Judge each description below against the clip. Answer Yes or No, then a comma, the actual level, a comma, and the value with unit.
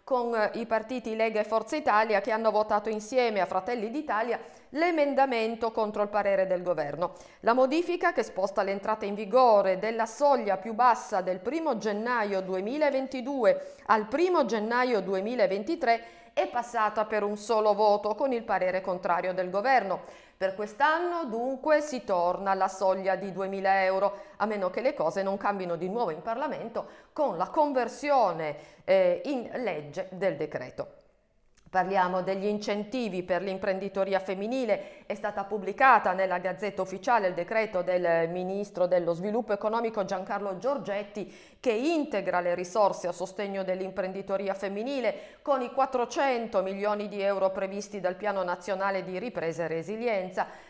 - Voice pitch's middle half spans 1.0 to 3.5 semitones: No, average, 4.0 semitones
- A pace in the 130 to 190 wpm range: Yes, average, 145 wpm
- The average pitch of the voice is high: Yes, high, 205 Hz